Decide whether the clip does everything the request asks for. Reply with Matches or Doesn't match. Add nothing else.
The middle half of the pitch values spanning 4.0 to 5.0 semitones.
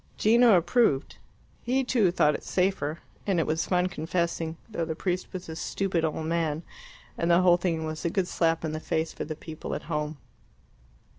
Doesn't match